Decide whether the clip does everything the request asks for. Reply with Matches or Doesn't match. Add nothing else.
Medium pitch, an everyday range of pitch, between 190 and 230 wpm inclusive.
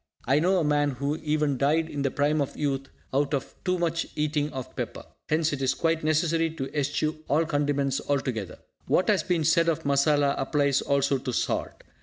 Doesn't match